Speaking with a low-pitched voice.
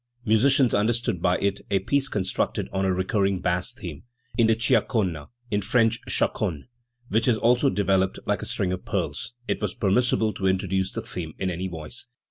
Yes: very low, 95 Hz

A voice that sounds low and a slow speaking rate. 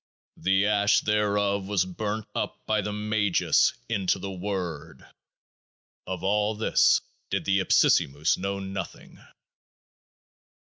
Yes: low, 100 Hz; slow, 115 wpm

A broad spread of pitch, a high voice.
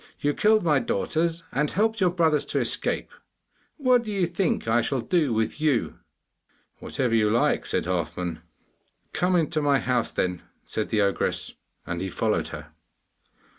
No: wide, 7.6 semitones; medium, 145 Hz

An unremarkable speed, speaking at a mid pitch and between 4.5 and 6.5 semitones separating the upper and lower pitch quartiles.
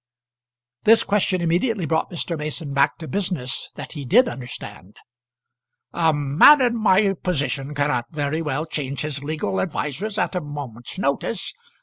Yes: average, 145 wpm; medium, 155 Hz; average, 4.9 semitones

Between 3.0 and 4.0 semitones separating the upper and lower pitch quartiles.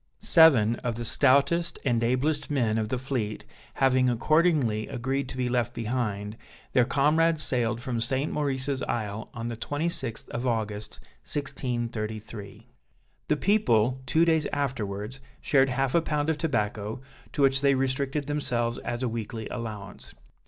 Yes: average, 3.7 semitones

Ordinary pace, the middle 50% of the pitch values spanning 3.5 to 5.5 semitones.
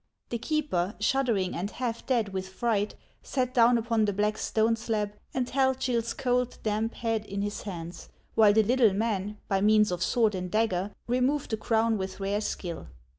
No: average, 180 wpm; average, 3.0 semitones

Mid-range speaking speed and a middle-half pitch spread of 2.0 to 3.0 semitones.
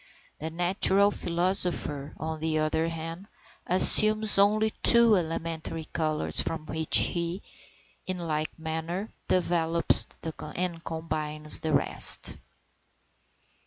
No: slow, 100 wpm; narrow, 2.6 semitones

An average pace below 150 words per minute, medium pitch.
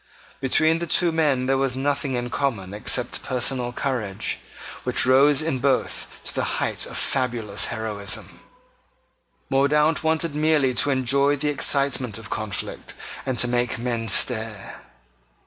No: average, 140 wpm; low, 130 Hz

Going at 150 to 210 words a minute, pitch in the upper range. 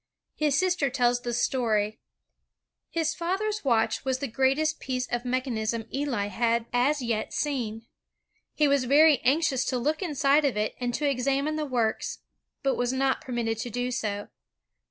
Yes: average, 155 wpm; very high, 255 Hz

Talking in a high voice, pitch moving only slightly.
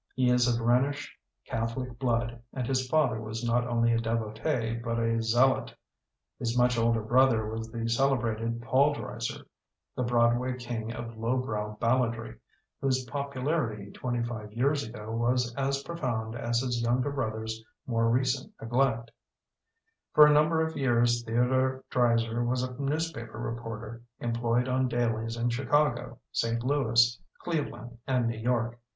No: low, 120 Hz; narrow, 2.1 semitones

